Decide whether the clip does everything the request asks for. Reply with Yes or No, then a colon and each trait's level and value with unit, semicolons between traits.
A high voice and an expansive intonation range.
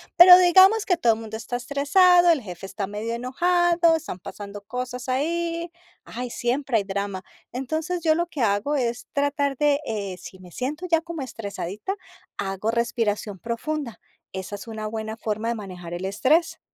Yes: high, 245 Hz; wide, 7.3 semitones